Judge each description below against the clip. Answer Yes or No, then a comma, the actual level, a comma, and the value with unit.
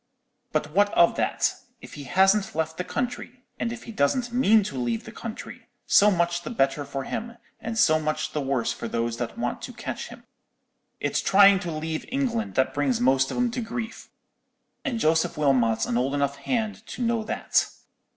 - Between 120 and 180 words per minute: No, average, 195 wpm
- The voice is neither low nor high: Yes, medium, 170 Hz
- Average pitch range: No, wide, 8.6 semitones